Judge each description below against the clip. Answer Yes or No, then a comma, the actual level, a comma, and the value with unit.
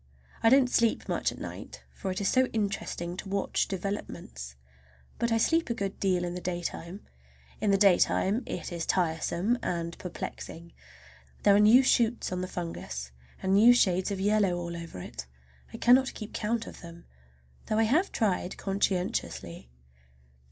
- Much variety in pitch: No, average, 4.2 semitones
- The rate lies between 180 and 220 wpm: No, average, 170 wpm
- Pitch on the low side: No, high, 195 Hz